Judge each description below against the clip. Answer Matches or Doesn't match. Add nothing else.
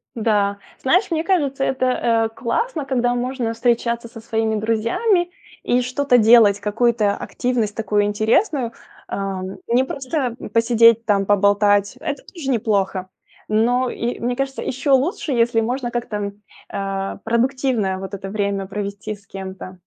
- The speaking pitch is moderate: Doesn't match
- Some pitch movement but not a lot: Matches